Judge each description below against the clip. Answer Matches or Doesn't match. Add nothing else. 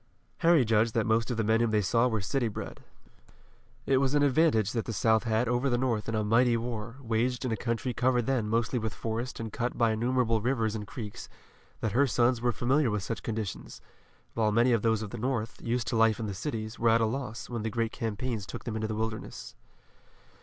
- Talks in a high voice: Doesn't match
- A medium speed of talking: Doesn't match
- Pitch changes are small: Matches